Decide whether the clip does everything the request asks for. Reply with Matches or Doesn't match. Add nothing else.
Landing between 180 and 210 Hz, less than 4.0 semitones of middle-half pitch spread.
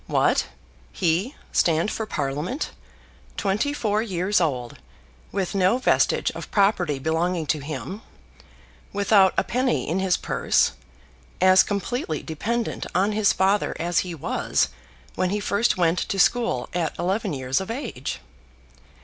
Doesn't match